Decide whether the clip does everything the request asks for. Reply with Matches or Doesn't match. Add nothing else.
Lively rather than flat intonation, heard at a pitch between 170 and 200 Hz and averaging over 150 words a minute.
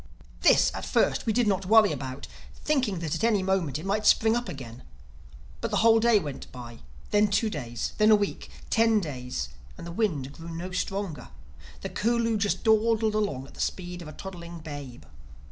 Matches